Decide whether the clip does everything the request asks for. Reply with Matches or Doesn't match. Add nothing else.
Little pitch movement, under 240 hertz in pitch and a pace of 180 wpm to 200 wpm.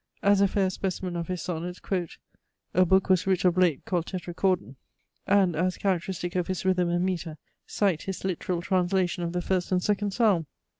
Matches